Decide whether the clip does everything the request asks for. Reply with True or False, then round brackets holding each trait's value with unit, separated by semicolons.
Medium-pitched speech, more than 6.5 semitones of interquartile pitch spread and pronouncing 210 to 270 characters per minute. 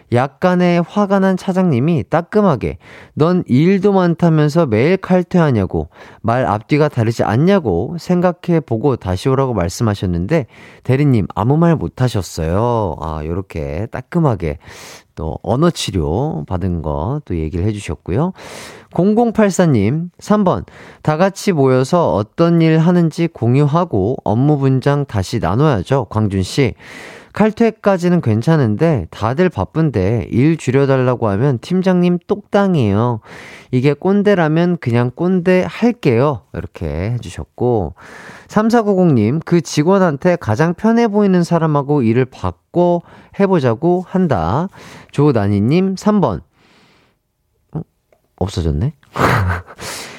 True (145 Hz; 8.1 semitones; 245 characters per minute)